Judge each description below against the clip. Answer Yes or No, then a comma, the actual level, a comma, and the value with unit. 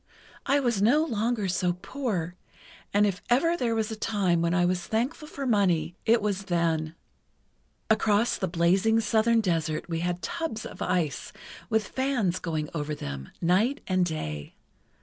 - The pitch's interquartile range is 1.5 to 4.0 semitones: No, average, 5.0 semitones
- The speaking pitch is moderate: No, high, 195 Hz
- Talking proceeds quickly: No, average, 160 wpm